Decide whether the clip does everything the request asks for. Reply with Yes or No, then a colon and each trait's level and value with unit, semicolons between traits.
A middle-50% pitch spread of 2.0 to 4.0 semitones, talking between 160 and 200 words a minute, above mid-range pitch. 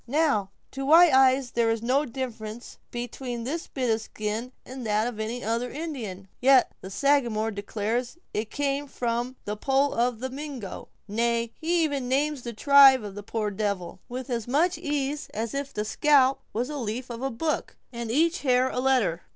Yes: average, 3.7 semitones; average, 190 wpm; very high, 250 Hz